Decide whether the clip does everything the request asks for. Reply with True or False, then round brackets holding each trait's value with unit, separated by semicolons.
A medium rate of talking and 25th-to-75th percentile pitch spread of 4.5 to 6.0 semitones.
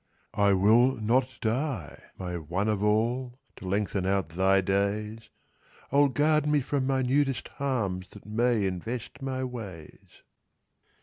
False (130 wpm; 5.0 semitones)